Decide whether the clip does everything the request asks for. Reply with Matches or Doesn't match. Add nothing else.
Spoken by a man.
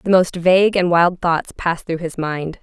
Doesn't match